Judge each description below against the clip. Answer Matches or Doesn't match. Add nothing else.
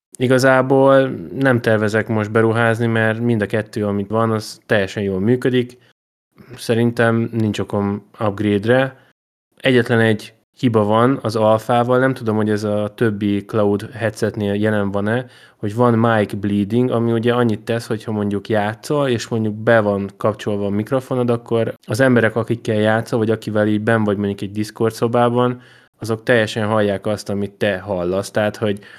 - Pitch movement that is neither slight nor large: Doesn't match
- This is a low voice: Matches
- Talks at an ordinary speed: Doesn't match